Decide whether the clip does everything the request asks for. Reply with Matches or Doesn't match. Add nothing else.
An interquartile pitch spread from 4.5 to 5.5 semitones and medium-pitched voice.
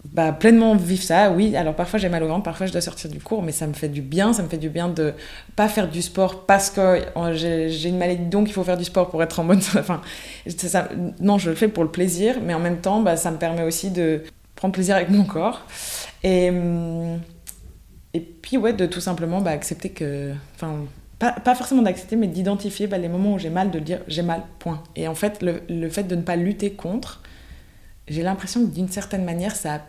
Doesn't match